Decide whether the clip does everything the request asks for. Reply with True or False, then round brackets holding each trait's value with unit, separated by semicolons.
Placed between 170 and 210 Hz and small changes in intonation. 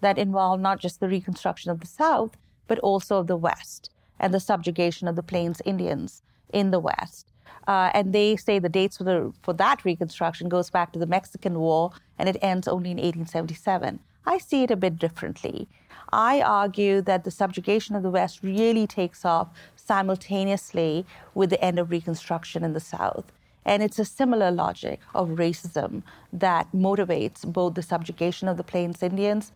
True (185 Hz; 2.1 semitones)